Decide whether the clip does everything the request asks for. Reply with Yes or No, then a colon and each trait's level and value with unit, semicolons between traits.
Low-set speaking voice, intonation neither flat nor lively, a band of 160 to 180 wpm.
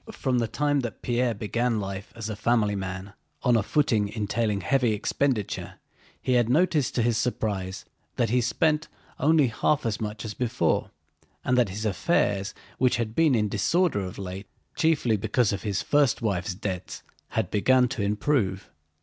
Yes: low, 115 Hz; average, 3.9 semitones; average, 165 wpm